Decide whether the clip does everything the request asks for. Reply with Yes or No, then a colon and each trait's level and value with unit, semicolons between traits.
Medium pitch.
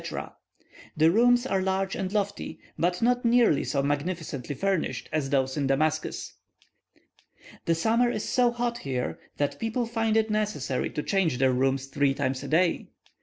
Yes: medium, 180 Hz